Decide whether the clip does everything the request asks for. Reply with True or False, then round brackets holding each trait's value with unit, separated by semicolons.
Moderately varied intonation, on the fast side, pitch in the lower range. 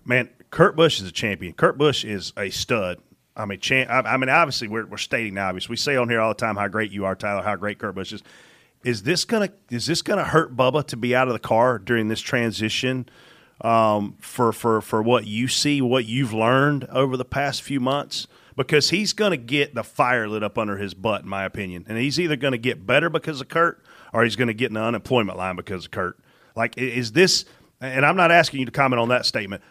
True (4.2 semitones; 240 wpm; 125 Hz)